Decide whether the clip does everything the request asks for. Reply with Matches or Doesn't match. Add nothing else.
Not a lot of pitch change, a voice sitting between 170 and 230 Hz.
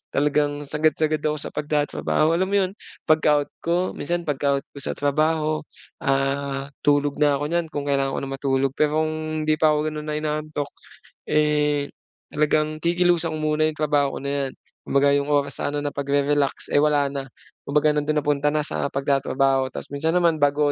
Doesn't match